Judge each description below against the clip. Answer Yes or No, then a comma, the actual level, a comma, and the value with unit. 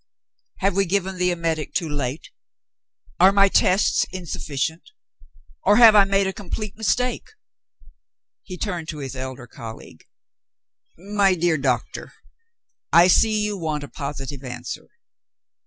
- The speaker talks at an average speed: No, slow, 130 wpm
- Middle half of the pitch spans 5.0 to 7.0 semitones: Yes, wide, 5.4 semitones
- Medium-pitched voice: Yes, medium, 175 Hz